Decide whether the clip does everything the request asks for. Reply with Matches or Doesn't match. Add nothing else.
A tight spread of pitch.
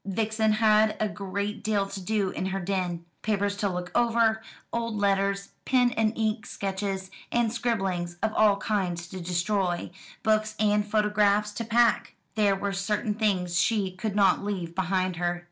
Matches